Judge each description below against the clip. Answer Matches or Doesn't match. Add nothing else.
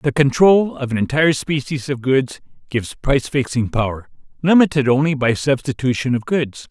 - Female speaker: Doesn't match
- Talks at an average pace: Matches